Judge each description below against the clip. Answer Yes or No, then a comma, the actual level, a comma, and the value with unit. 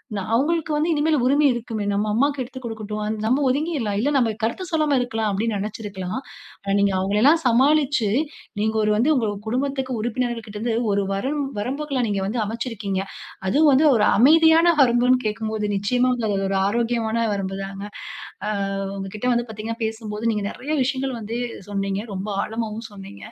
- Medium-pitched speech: No, high, 230 Hz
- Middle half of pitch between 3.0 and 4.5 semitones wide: Yes, average, 4.1 semitones